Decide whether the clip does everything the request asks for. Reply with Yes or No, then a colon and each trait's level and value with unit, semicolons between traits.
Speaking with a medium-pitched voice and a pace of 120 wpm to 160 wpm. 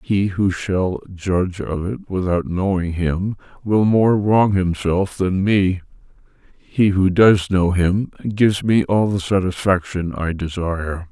No: very low, 95 Hz; average, 145 wpm